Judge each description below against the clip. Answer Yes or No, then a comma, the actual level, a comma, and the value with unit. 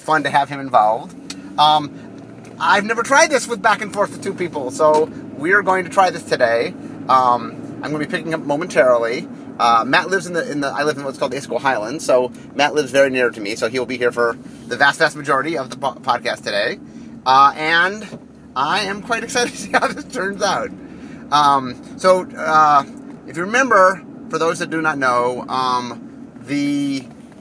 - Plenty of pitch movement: Yes, wide, 8.5 semitones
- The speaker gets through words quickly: Yes, fast, 210 wpm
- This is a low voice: No, medium, 170 Hz